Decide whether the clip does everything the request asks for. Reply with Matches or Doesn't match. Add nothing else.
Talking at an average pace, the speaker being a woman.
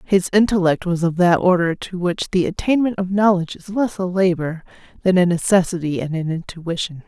Matches